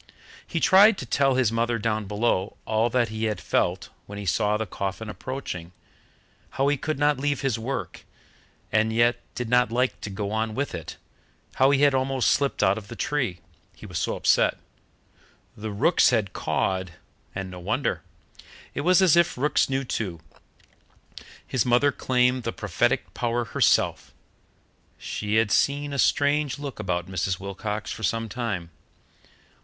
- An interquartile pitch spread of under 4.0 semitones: No, average, 4.8 semitones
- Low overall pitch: Yes, low, 115 Hz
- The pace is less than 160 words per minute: No, average, 165 wpm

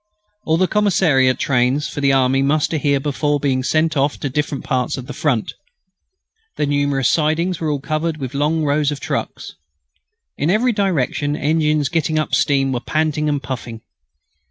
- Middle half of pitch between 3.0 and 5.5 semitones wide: No, narrow, 2.5 semitones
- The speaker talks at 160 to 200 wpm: Yes, average, 170 wpm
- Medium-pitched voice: Yes, medium, 145 Hz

